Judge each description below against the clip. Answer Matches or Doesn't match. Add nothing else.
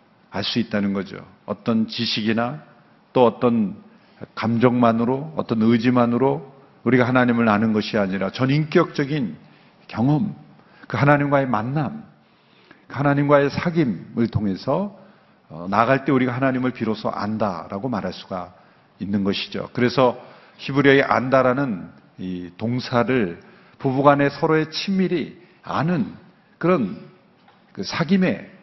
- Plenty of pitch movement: Matches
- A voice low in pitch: Matches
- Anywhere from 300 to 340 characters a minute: Doesn't match